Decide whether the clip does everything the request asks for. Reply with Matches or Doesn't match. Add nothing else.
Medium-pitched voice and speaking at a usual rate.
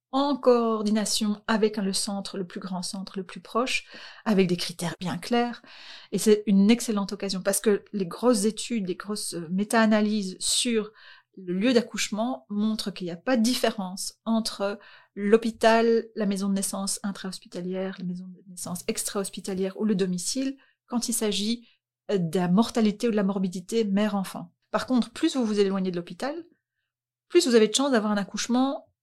Doesn't match